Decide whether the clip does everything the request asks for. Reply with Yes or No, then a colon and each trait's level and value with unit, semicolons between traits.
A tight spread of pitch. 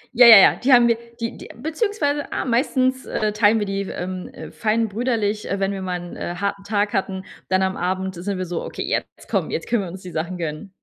No: average, 3.8 semitones